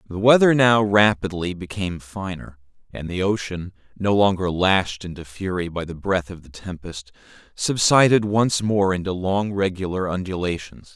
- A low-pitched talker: Yes, very low, 95 Hz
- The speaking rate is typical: Yes, average, 150 wpm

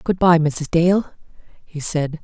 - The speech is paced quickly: No, average, 160 wpm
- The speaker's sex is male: No, female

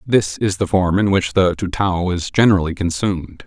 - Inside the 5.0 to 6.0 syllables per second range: Yes, 5.1 syllables/s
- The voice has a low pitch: Yes, very low, 95 Hz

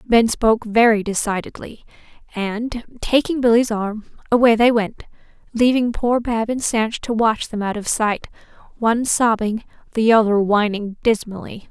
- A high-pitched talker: Yes, high, 225 Hz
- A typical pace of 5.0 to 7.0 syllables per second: No, 4.6 syllables/s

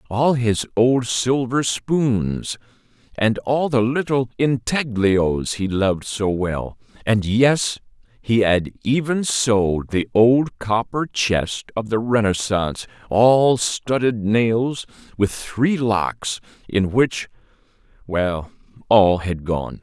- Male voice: Yes, male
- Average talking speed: No, slow, 120 wpm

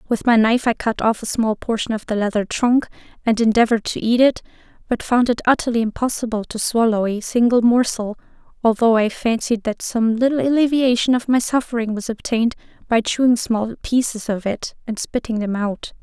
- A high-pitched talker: Yes, high, 230 Hz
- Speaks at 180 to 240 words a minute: Yes, average, 185 wpm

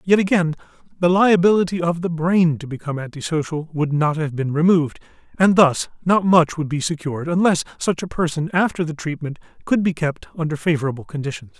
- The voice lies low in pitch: No, medium, 165 Hz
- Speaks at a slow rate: No, average, 180 wpm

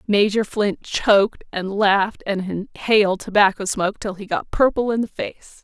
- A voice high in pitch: Yes, high, 200 Hz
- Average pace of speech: Yes, average, 170 wpm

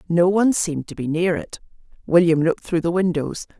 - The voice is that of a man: No, female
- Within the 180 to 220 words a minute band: Yes, average, 200 wpm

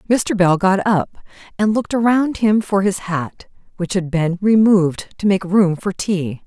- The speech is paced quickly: No, average, 185 wpm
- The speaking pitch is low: No, high, 190 Hz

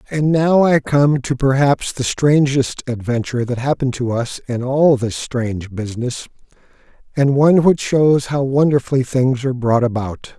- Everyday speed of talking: Yes, average, 160 wpm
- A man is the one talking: Yes, male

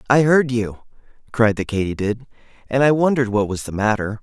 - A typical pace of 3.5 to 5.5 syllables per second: No, 5.8 syllables/s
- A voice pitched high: No, low, 115 Hz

